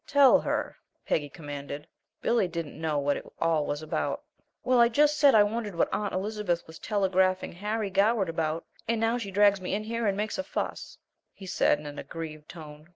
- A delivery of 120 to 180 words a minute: No, average, 200 wpm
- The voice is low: No, high, 190 Hz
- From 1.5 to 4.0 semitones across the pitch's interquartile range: No, wide, 5.4 semitones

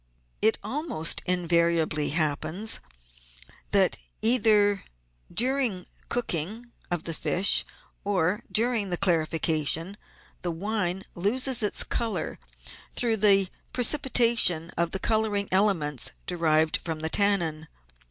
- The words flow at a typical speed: No, slow, 115 wpm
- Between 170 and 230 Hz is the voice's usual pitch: Yes, high, 190 Hz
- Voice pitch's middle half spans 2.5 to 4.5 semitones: No, average, 5.1 semitones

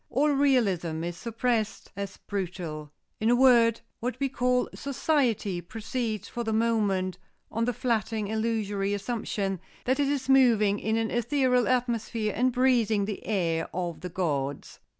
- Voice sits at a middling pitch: No, high, 220 Hz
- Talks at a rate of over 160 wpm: No, average, 150 wpm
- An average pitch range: Yes, average, 4.1 semitones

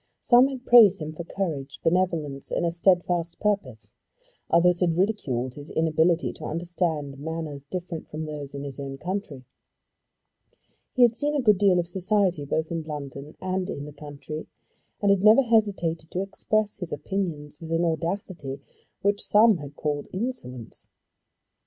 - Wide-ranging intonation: No, average, 4.9 semitones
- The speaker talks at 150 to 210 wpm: Yes, average, 160 wpm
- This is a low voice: No, medium, 170 Hz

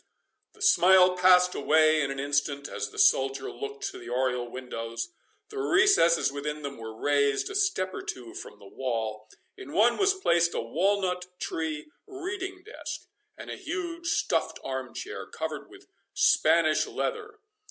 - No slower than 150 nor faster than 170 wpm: Yes, average, 160 wpm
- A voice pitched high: No, medium, 165 Hz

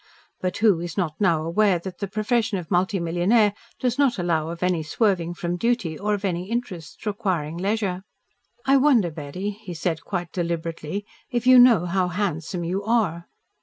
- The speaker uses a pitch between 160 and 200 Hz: Yes, medium, 185 Hz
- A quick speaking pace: No, average, 165 wpm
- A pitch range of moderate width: Yes, average, 3.9 semitones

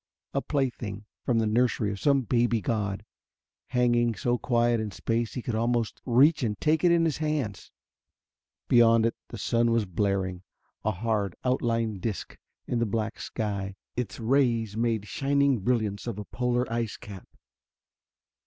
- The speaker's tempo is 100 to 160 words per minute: Yes, average, 155 wpm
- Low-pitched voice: Yes, low, 115 Hz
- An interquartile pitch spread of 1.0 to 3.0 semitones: Yes, average, 2.7 semitones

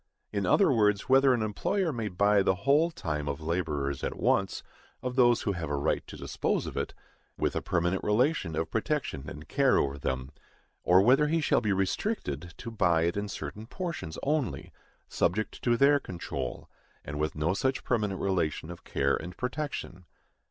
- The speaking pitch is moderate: No, low, 100 Hz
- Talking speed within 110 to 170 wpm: No, average, 180 wpm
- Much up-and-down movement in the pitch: Yes, wide, 8.0 semitones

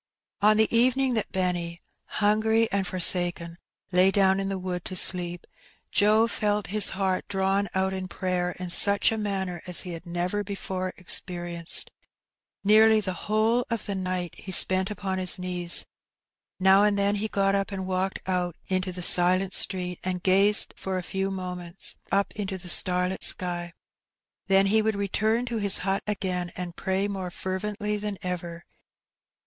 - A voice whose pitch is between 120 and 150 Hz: No, high, 190 Hz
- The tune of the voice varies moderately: No, narrow, 2.1 semitones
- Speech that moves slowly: No, average, 170 wpm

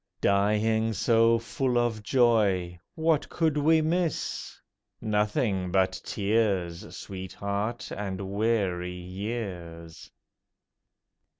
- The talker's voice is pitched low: Yes, low, 105 Hz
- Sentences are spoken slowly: Yes, slow, 85 wpm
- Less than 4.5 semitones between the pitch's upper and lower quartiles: Yes, average, 3.7 semitones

